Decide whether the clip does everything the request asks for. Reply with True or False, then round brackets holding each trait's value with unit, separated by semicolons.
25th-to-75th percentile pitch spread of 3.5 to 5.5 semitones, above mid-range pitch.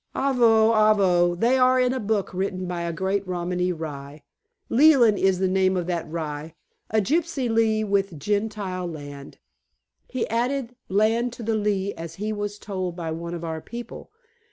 True (4.4 semitones; 200 Hz)